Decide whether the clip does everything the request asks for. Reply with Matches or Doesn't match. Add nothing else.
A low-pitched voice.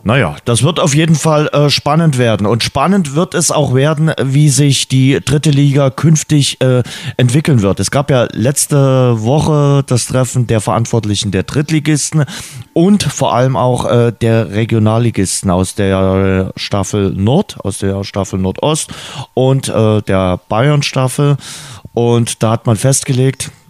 Matches